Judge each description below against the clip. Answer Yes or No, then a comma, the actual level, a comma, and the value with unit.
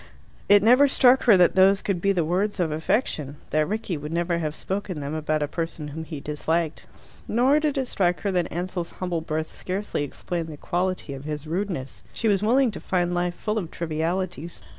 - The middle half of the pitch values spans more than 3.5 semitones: Yes, average, 4.1 semitones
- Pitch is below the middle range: No, medium, 175 Hz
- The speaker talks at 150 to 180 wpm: No, fast, 205 wpm